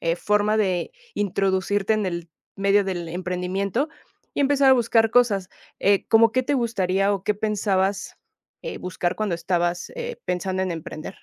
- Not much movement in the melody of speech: No, average, 3.2 semitones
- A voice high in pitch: Yes, high, 195 Hz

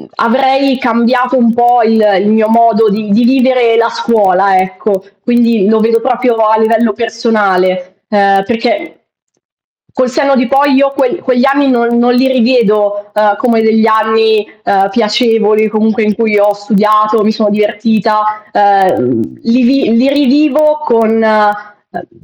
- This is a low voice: No, high, 225 Hz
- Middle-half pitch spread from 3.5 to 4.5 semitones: No, narrow, 2.6 semitones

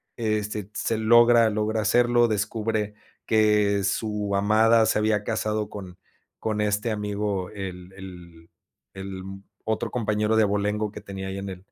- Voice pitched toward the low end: Yes, low, 105 Hz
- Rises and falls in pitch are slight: Yes, narrow, 1.7 semitones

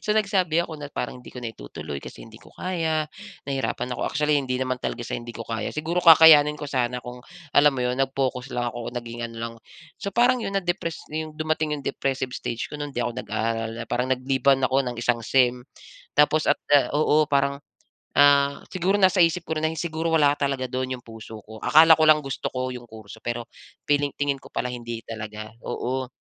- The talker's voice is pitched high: No, low, 135 Hz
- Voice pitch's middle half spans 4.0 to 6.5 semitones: Yes, average, 4.3 semitones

